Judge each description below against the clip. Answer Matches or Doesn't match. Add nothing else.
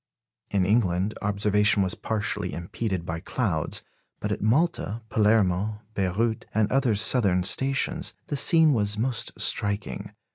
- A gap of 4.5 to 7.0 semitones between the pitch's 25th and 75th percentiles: Doesn't match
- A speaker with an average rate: Doesn't match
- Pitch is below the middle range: Matches